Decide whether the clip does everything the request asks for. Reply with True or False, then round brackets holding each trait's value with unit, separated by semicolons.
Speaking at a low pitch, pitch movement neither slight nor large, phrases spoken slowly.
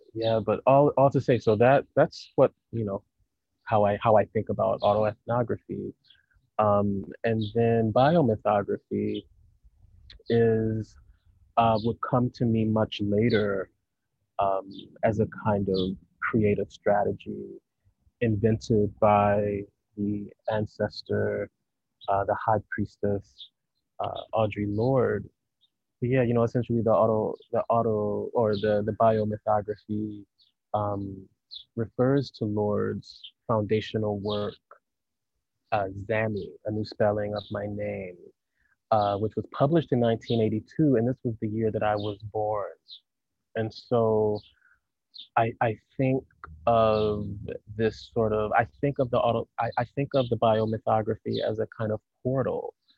False (110 Hz; 2.0 semitones; 130 wpm)